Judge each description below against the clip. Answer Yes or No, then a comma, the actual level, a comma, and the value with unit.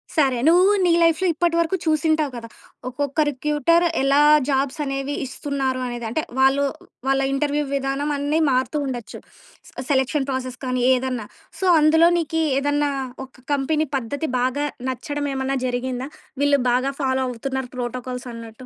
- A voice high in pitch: Yes, very high, 275 Hz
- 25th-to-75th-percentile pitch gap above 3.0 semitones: No, narrow, 2.6 semitones